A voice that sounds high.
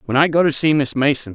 No: medium, 145 Hz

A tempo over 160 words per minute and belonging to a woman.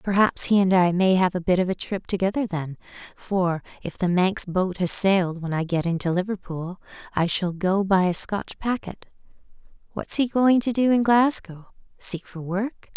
Yes: average, 190 wpm; female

